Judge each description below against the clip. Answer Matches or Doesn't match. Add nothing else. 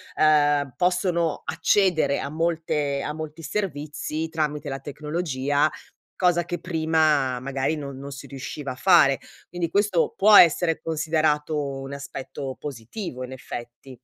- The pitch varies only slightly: Doesn't match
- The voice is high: Doesn't match